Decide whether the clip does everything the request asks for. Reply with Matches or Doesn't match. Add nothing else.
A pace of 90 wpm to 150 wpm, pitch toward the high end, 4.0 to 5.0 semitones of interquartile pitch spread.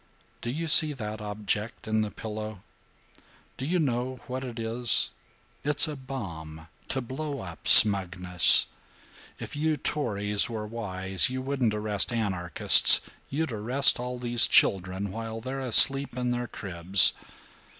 Doesn't match